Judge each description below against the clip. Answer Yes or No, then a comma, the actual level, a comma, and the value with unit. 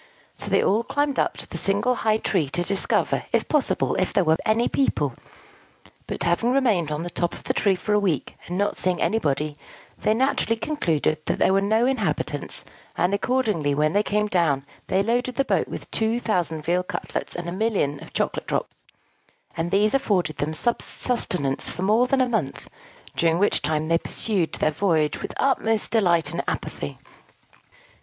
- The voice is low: No, high, 195 Hz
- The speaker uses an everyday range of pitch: No, wide, 5.8 semitones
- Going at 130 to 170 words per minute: No, average, 185 wpm